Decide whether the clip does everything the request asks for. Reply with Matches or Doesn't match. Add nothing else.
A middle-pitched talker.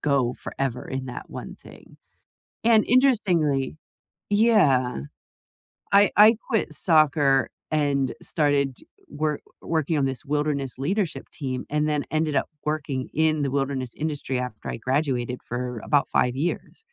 Matches